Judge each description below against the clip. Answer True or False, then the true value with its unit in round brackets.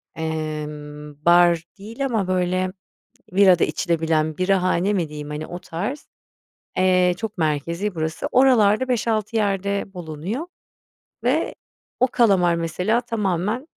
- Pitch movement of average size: True (4.6 semitones)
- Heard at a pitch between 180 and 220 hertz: True (185 Hz)